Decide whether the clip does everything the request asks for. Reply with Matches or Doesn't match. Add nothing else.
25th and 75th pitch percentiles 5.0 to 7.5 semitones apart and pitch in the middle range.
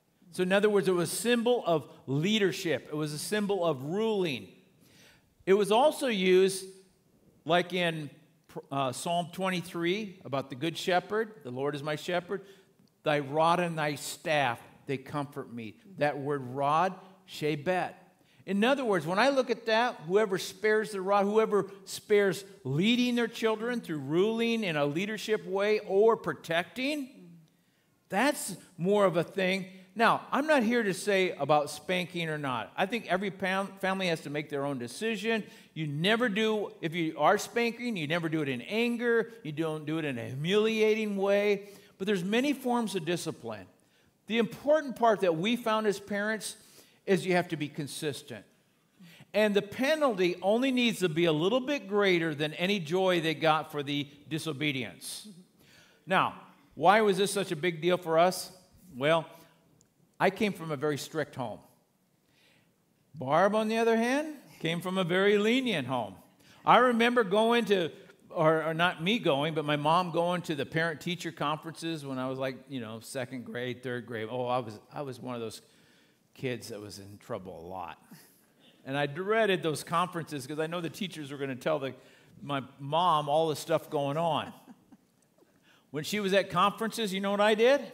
Matches